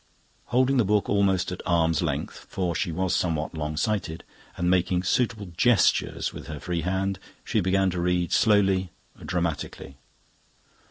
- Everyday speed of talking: Yes, average, 150 wpm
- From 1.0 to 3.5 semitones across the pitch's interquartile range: Yes, narrow, 2.6 semitones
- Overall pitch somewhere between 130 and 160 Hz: No, very low, 90 Hz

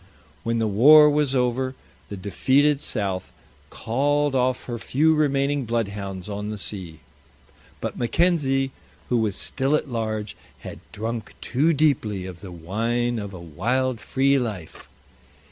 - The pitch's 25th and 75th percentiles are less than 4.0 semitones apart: No, average, 5.0 semitones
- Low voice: Yes, low, 120 Hz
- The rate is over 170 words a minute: No, average, 140 wpm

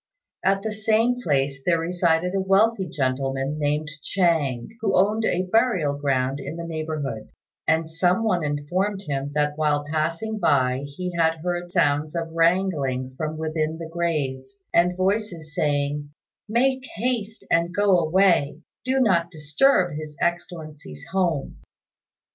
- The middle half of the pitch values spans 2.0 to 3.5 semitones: No, average, 4.4 semitones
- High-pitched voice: No, medium, 165 Hz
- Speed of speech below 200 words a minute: Yes, average, 140 wpm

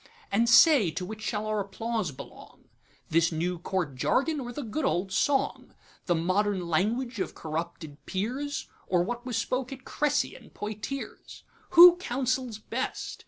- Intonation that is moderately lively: No, wide, 6.2 semitones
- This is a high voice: Yes, high, 215 Hz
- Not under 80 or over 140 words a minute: Yes, slow, 135 wpm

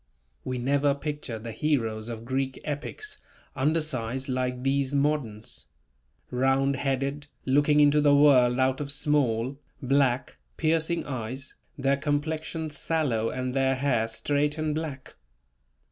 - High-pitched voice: No, low, 135 Hz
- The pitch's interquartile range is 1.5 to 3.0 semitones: Yes, narrow, 2.5 semitones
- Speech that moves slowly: Yes, slow, 125 wpm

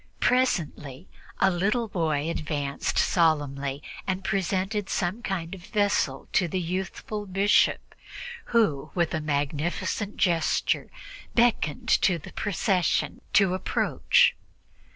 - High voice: No, medium, 180 Hz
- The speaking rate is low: Yes, slow, 110 wpm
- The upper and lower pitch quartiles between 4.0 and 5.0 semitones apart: Yes, average, 4.5 semitones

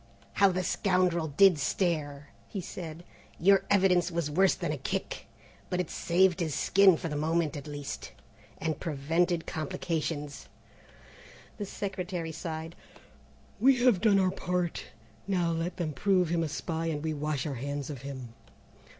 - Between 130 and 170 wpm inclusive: Yes, average, 155 wpm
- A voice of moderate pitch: Yes, medium, 170 Hz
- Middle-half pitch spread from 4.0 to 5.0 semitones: No, average, 3.4 semitones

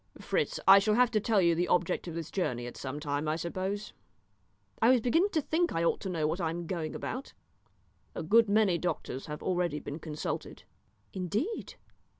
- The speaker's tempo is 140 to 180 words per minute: No, average, 195 wpm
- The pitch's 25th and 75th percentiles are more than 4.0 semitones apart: Yes, average, 5.1 semitones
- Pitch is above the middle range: No, medium, 180 Hz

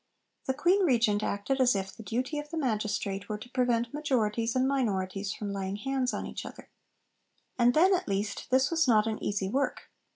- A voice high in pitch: Yes, high, 235 Hz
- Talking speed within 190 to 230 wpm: Yes, average, 195 wpm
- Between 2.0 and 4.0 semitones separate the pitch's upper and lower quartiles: No, average, 4.6 semitones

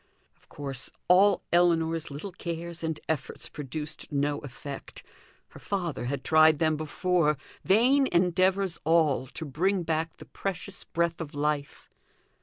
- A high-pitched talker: No, medium, 160 Hz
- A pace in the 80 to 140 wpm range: Yes, slow, 135 wpm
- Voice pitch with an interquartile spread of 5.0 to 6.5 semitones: No, average, 3.2 semitones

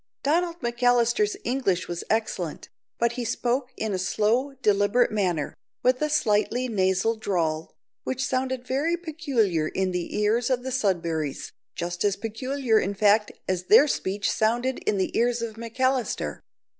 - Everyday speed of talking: Yes, average, 155 wpm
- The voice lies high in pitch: Yes, high, 225 Hz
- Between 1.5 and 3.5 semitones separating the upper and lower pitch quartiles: No, average, 4.6 semitones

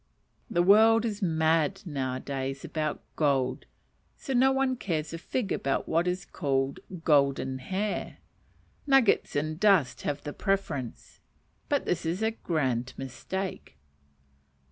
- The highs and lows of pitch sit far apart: Yes, wide, 6.3 semitones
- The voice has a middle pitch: Yes, medium, 160 Hz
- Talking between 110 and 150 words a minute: Yes, slow, 135 wpm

